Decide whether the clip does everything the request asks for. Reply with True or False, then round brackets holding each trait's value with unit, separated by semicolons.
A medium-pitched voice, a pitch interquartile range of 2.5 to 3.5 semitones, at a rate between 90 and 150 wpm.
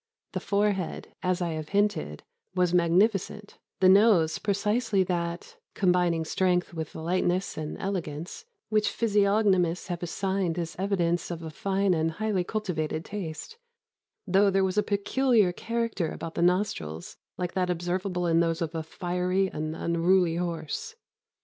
True (180 Hz; 3.0 semitones; 145 wpm)